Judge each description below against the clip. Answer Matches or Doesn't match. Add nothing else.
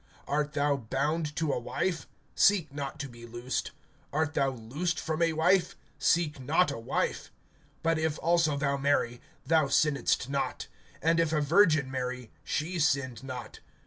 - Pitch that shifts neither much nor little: Matches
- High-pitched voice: Doesn't match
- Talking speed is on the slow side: Doesn't match